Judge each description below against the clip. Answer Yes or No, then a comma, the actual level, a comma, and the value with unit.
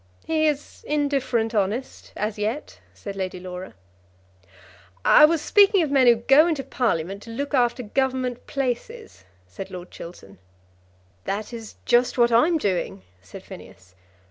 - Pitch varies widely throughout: Yes, wide, 6.0 semitones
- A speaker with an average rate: Yes, average, 145 wpm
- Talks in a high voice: Yes, high, 240 Hz